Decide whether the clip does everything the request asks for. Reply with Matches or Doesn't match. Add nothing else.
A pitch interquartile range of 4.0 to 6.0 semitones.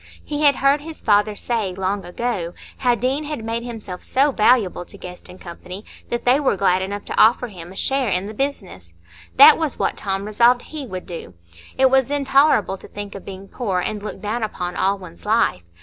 Matches